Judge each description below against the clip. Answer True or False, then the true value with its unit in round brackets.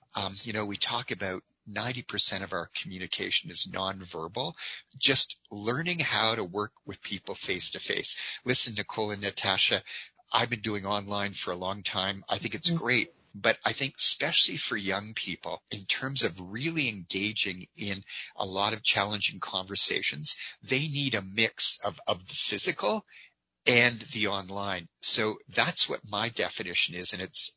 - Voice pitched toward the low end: True (105 Hz)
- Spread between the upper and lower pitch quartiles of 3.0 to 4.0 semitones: True (3.6 semitones)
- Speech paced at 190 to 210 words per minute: False (165 wpm)